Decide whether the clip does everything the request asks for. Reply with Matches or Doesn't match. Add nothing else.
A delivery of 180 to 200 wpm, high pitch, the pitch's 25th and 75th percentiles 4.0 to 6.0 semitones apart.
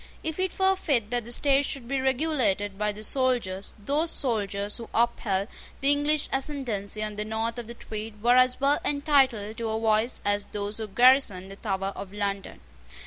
Matches